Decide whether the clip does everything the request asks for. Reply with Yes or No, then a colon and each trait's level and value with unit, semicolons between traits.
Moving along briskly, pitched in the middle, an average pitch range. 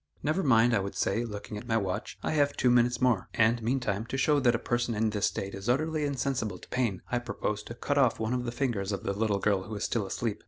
No: fast, 265 wpm; low, 115 Hz; average, 3.4 semitones